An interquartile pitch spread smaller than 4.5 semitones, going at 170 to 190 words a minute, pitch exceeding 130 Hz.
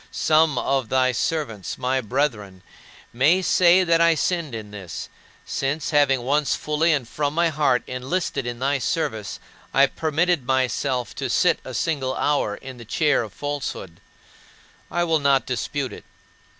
No: average, 3.9 semitones; average, 155 wpm; medium, 140 Hz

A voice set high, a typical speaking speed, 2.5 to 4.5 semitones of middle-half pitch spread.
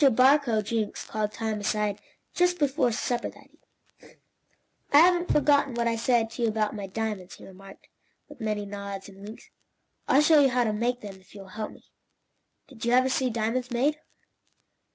Yes: high, 230 Hz; average, 190 wpm; average, 3.8 semitones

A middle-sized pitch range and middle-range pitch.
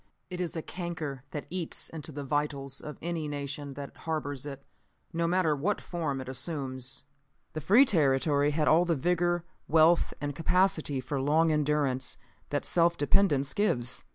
Yes: average, 3.3 semitones; medium, 150 Hz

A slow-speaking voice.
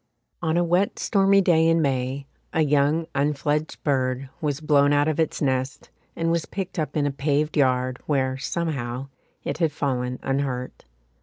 No: average, 165 wpm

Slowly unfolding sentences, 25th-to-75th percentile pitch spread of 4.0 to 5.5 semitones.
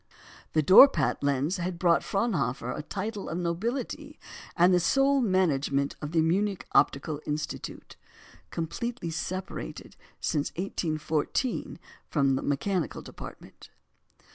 Yes: slow, 115 wpm; average, 4.9 semitones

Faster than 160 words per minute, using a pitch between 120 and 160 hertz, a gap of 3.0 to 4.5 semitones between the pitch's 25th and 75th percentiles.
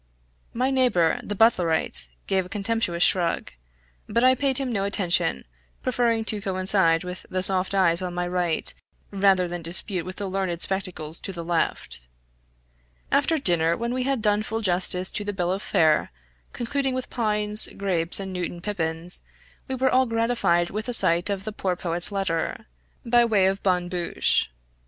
No: average, 170 wpm; high, 190 Hz; average, 4.2 semitones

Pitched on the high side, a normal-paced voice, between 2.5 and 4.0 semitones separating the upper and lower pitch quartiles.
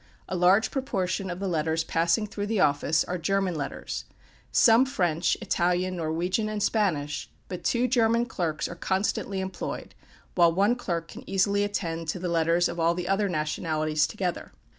No: medium, 180 Hz; average, 170 wpm; average, 3.5 semitones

